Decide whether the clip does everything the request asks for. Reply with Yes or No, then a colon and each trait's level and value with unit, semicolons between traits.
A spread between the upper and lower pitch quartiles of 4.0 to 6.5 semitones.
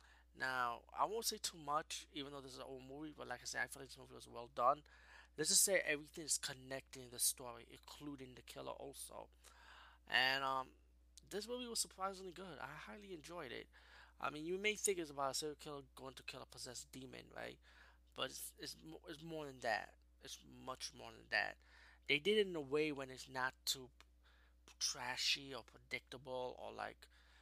Yes: average, 4.5 semitones